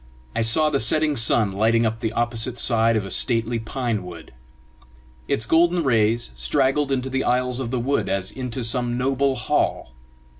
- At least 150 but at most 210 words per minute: Yes, average, 175 wpm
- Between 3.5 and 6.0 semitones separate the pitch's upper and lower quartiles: No, average, 2.9 semitones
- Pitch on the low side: Yes, low, 120 Hz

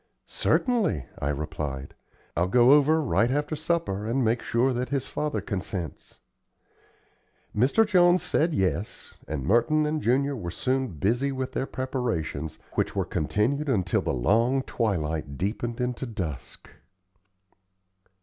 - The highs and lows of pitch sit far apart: Yes, wide, 7.4 semitones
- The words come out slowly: Yes, slow, 130 wpm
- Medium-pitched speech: No, low, 120 Hz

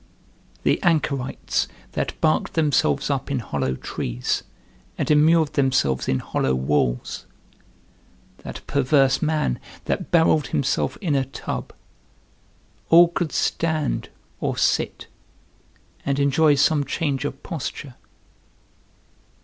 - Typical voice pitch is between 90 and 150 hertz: Yes, medium, 140 Hz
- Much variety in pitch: No, average, 3.6 semitones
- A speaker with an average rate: No, slow, 110 wpm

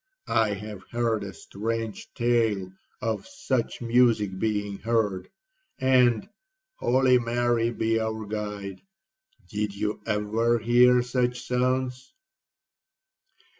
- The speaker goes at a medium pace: No, slow, 95 wpm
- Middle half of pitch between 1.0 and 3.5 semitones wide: Yes, average, 3.0 semitones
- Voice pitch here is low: Yes, low, 115 Hz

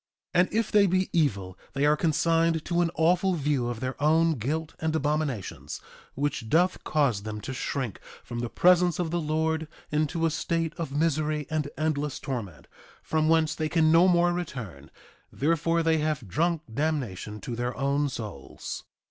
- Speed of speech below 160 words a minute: No, average, 175 wpm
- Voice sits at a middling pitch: Yes, medium, 155 Hz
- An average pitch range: Yes, average, 3.6 semitones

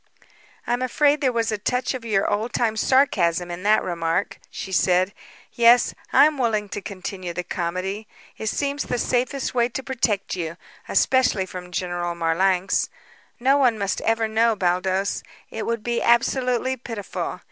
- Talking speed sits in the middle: Yes, average, 160 wpm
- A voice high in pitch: Yes, high, 215 Hz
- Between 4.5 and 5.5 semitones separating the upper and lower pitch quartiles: Yes, average, 5.0 semitones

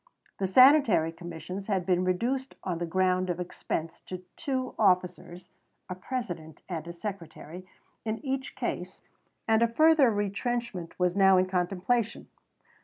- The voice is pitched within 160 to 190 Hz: Yes, medium, 185 Hz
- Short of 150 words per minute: Yes, average, 140 wpm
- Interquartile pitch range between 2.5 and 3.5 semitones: No, average, 4.7 semitones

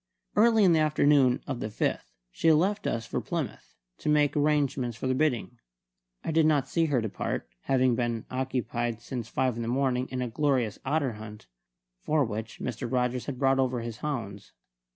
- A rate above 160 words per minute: Yes, average, 185 wpm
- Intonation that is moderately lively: Yes, average, 3.8 semitones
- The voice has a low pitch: Yes, low, 130 Hz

